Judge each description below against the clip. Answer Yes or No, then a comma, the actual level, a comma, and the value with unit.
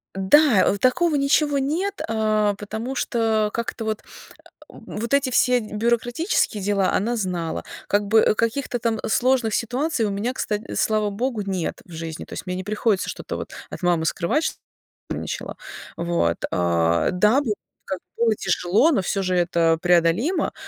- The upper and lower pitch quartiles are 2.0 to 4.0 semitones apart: No, average, 4.9 semitones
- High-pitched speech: Yes, high, 215 Hz